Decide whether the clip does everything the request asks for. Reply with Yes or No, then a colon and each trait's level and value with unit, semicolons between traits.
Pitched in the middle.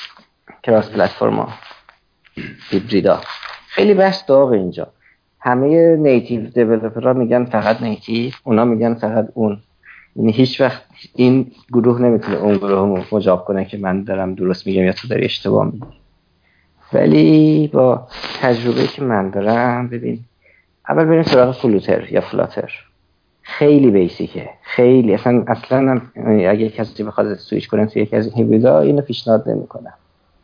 No: low, 115 Hz